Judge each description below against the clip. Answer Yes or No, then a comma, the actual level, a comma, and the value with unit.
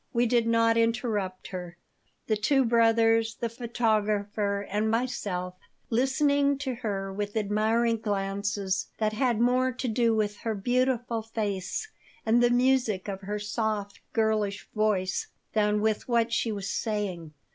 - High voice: Yes, high, 220 Hz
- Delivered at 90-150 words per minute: Yes, average, 140 wpm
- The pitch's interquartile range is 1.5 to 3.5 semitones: Yes, narrow, 2.5 semitones